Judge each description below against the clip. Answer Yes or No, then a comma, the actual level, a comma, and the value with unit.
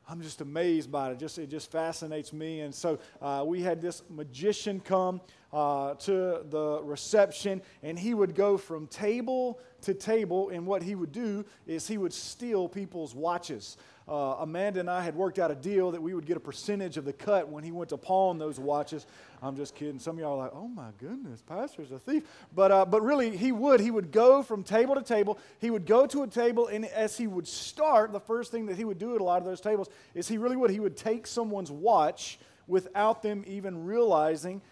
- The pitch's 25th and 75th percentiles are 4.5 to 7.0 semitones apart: Yes, average, 5.2 semitones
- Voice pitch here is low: No, high, 190 Hz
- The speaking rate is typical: No, fast, 225 wpm